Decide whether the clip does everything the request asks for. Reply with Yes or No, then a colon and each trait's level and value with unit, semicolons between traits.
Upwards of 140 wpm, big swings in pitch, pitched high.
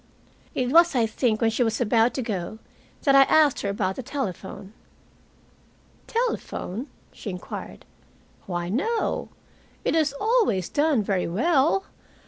No: slow, 135 wpm; wide, 7.0 semitones; high, 240 Hz